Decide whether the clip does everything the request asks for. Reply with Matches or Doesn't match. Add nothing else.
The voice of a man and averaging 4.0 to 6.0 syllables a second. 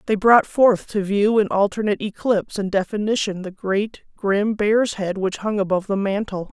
Doesn't match